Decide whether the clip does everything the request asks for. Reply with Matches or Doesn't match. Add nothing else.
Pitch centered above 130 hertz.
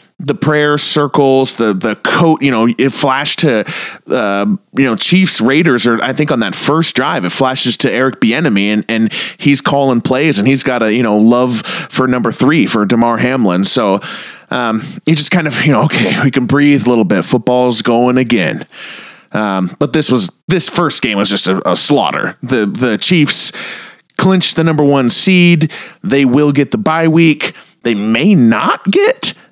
Matches